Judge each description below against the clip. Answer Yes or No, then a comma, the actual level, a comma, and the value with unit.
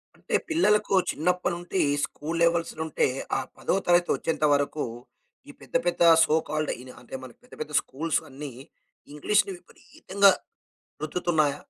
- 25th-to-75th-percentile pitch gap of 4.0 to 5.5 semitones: No, average, 3.1 semitones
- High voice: No, medium, 165 Hz